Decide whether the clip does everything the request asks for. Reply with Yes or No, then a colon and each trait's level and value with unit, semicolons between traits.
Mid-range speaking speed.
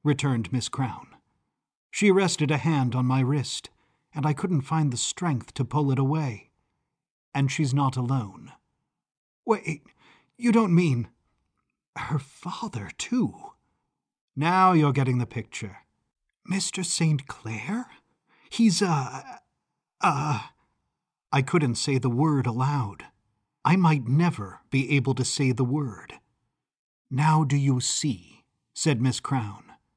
No: slow, 130 wpm